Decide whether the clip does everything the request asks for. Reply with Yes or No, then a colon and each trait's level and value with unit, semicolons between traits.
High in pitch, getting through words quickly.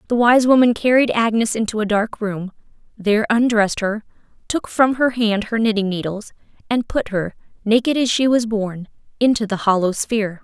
No: high, 220 Hz; average, 180 wpm